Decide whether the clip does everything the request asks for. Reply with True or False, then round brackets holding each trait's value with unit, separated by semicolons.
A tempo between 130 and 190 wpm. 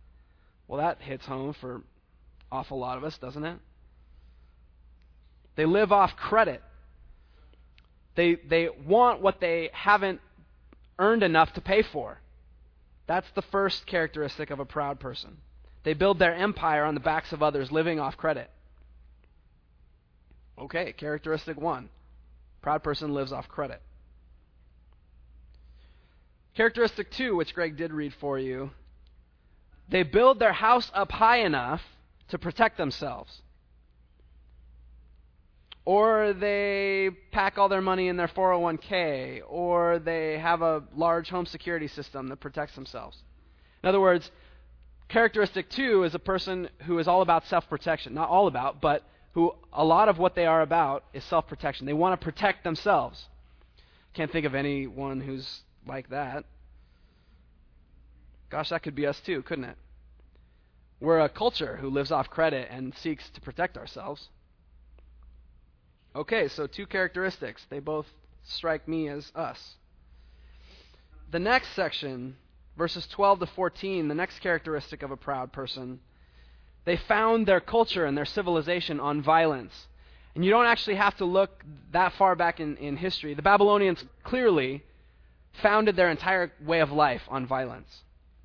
True (140 wpm)